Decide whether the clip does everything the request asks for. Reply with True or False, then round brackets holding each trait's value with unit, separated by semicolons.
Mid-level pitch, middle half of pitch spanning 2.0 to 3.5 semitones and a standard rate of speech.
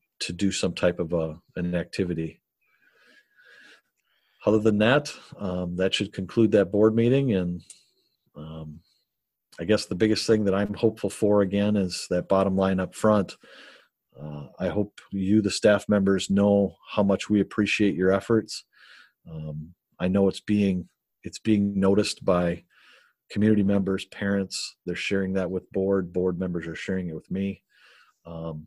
False (95 Hz; 2.6 semitones; 155 wpm)